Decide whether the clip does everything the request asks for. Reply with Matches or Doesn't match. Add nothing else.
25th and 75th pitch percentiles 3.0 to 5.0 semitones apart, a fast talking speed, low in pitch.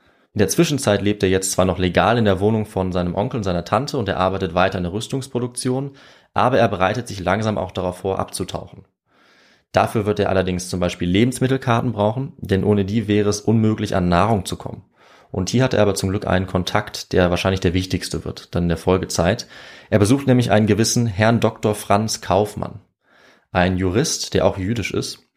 Matches